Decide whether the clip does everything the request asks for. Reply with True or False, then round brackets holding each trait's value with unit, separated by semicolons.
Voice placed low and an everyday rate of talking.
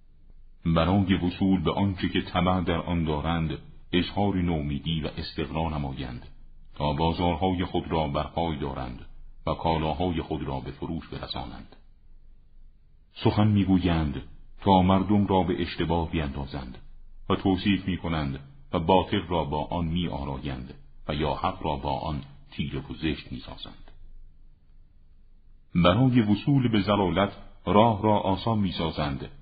True (85 Hz; 130 wpm)